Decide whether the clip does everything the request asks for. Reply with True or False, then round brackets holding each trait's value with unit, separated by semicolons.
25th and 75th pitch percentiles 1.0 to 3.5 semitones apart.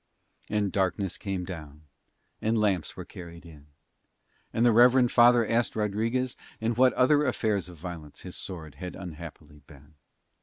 False (5.6 semitones)